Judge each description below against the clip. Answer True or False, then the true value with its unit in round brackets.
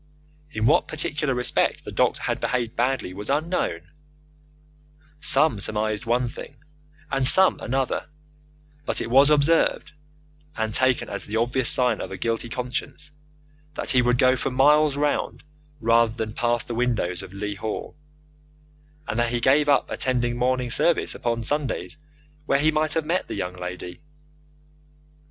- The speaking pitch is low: True (125 Hz)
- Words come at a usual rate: True (155 wpm)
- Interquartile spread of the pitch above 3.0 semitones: True (3.8 semitones)